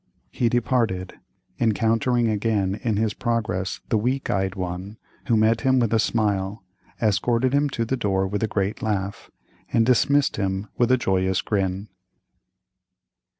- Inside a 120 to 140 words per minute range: No, average, 150 wpm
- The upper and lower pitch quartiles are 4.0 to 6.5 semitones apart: No, average, 3.5 semitones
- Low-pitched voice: Yes, low, 110 Hz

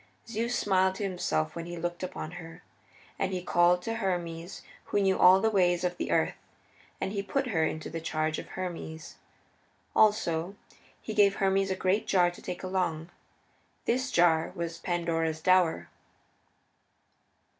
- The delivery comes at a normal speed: Yes, average, 155 wpm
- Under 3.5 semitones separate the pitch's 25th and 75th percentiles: Yes, average, 2.7 semitones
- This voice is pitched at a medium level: Yes, medium, 180 Hz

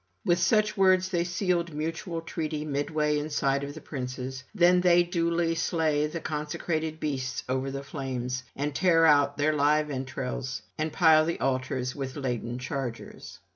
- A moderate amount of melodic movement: Yes, average, 3.7 semitones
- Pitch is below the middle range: No, medium, 150 Hz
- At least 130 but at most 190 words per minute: Yes, average, 160 wpm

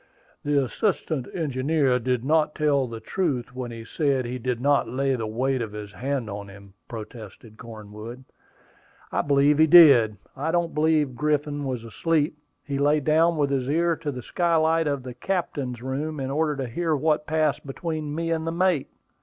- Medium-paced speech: Yes, average, 180 wpm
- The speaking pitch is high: No, medium, 140 Hz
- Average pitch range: Yes, average, 4.0 semitones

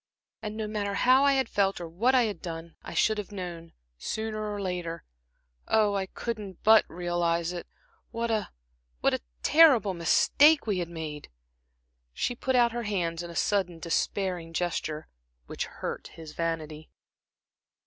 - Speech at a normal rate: Yes, average, 160 wpm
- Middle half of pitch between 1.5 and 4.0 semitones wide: No, average, 4.6 semitones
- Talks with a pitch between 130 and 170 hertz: No, high, 190 Hz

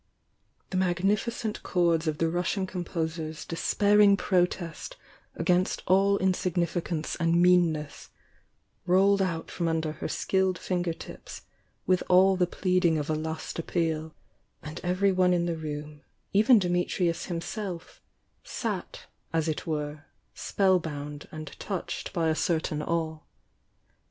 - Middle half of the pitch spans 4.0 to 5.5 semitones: No, narrow, 2.6 semitones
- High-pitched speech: No, medium, 175 Hz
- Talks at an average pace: No, slow, 130 wpm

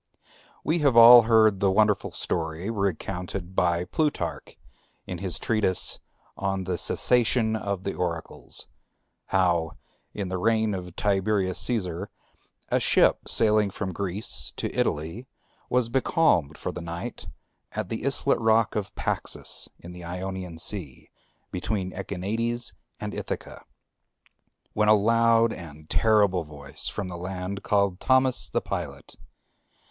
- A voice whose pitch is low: Yes, low, 100 Hz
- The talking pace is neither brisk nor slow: No, slow, 130 wpm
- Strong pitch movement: No, average, 3.8 semitones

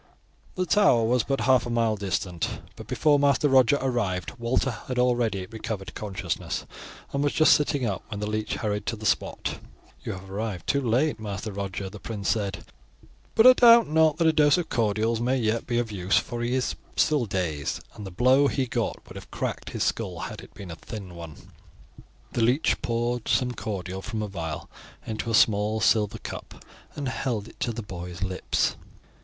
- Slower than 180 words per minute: No, average, 195 wpm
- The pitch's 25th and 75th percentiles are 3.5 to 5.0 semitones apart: Yes, average, 4.5 semitones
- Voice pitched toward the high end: No, low, 115 Hz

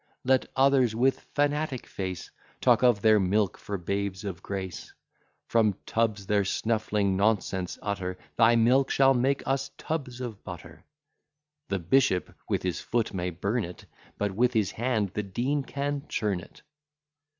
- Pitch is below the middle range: Yes, low, 110 Hz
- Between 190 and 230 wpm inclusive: No, average, 150 wpm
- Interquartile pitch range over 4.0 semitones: Yes, average, 4.8 semitones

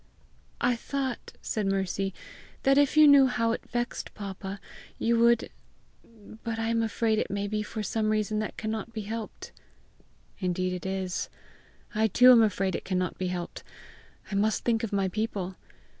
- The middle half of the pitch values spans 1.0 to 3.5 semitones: Yes, average, 3.0 semitones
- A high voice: Yes, high, 215 Hz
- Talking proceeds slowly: No, average, 170 wpm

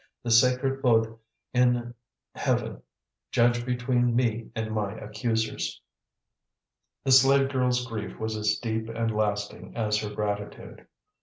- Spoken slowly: Yes, slow, 125 wpm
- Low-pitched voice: Yes, low, 115 Hz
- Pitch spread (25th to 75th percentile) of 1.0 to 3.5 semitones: Yes, narrow, 2.5 semitones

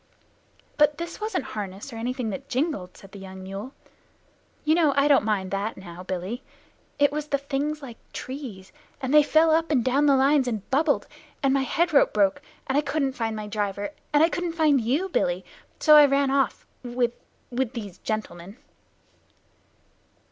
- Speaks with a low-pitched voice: No, very high, 265 Hz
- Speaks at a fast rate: No, average, 175 wpm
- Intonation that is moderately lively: No, wide, 5.8 semitones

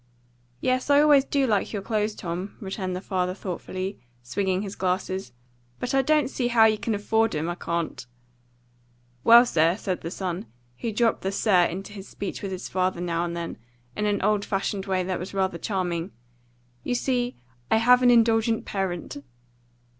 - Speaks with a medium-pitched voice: No, high, 195 Hz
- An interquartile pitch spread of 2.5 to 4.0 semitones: Yes, average, 3.7 semitones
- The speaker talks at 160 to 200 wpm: Yes, average, 180 wpm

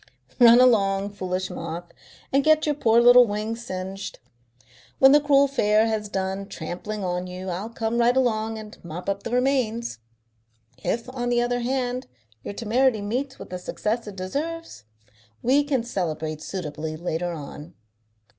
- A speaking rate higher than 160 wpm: No, average, 155 wpm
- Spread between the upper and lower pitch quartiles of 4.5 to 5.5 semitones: Yes, average, 5.0 semitones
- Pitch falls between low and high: No, high, 220 Hz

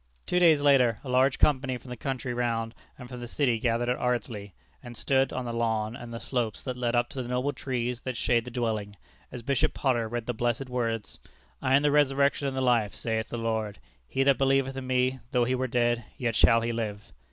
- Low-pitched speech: Yes, low, 125 Hz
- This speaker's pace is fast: Yes, fast, 230 wpm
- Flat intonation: Yes, narrow, 2.2 semitones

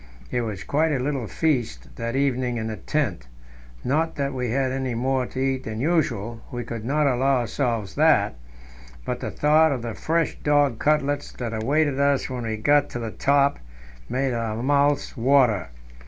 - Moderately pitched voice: No, low, 130 Hz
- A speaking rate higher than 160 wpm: Yes, average, 180 wpm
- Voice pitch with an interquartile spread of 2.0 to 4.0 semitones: Yes, average, 3.6 semitones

